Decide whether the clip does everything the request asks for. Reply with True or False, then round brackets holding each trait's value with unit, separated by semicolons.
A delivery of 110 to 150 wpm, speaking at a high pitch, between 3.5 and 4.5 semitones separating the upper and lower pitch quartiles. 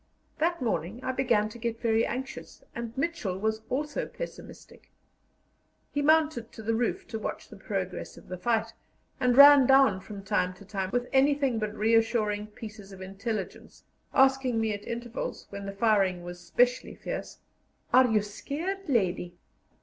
False (160 wpm; 225 Hz; 4.1 semitones)